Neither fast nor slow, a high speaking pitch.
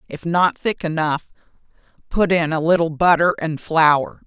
No: average, 155 wpm; medium, 160 Hz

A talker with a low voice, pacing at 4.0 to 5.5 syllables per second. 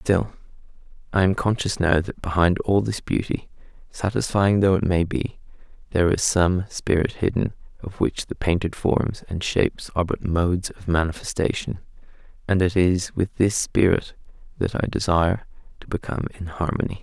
Yes: very low, 90 Hz; 5.1 syllables/s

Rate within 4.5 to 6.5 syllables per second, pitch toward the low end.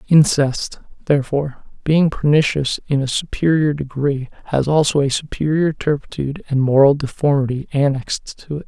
No: 5.3 syllables/s; medium, 145 Hz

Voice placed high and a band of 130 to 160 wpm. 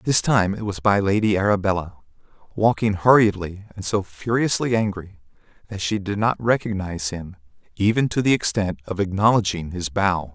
No: low, 100 Hz; average, 155 wpm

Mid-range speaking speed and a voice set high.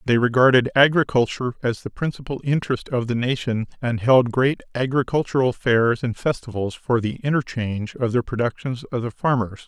No: average, 160 wpm; low, 125 Hz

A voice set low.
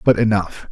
Yes: low, 105 Hz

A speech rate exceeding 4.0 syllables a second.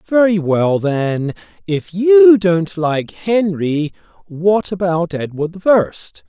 No: 3.1 syllables/s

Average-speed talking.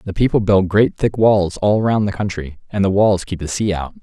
No: fast, 255 wpm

